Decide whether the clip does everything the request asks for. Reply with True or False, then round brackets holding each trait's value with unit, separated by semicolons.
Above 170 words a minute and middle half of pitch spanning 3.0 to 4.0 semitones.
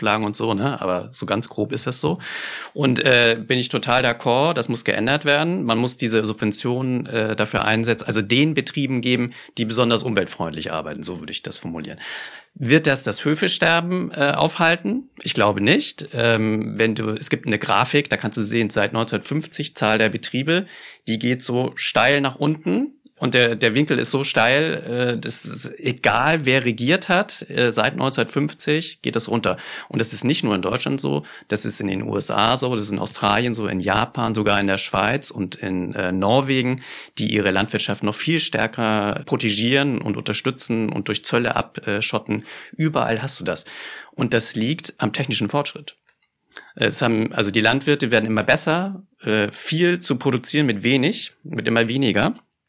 False (180 wpm; 4.7 semitones)